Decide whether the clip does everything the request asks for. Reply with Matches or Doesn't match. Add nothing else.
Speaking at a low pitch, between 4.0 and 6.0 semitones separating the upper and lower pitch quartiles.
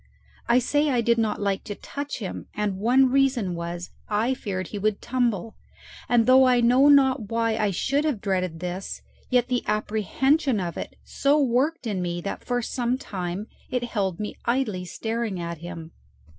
Doesn't match